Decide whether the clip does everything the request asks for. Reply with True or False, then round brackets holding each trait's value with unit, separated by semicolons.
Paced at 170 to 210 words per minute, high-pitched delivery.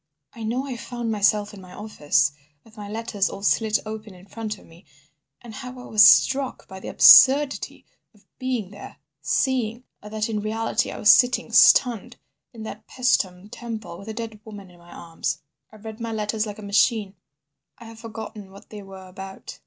True (190 wpm; 215 Hz)